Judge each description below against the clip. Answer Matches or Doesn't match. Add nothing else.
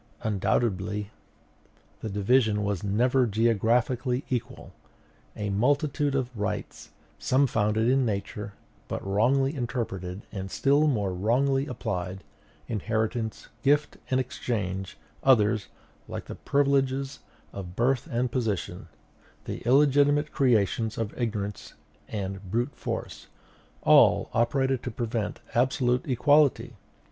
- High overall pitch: Doesn't match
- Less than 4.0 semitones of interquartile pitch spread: Doesn't match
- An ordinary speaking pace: Doesn't match